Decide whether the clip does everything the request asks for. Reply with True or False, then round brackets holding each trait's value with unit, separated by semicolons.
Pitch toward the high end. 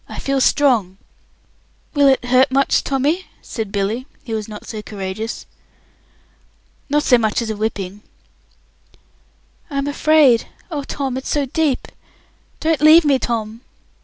True (255 Hz)